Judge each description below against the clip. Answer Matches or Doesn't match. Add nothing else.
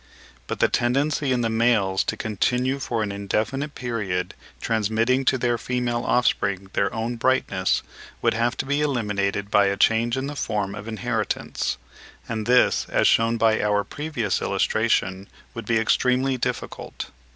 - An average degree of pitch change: Matches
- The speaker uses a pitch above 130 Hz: Doesn't match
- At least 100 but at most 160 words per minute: Matches